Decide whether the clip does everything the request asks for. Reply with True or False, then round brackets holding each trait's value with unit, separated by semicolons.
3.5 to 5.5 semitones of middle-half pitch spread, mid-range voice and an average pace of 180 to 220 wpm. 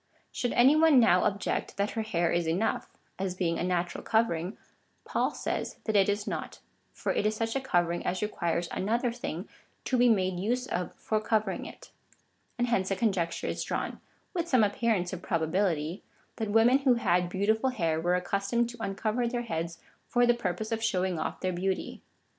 False (4.7 semitones; 205 Hz; 195 wpm)